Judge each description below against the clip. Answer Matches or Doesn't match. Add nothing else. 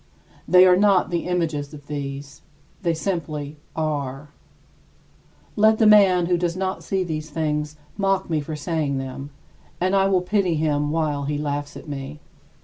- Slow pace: Doesn't match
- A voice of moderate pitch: Matches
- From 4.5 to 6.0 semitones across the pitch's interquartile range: Doesn't match